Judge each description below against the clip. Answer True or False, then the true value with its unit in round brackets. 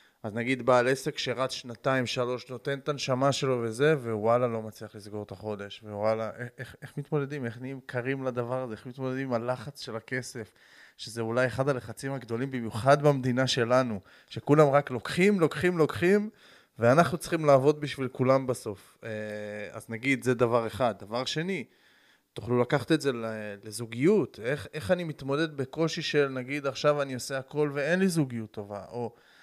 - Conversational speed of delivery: False (165 wpm)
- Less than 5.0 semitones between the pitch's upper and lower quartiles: True (3.9 semitones)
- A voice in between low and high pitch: False (130 Hz)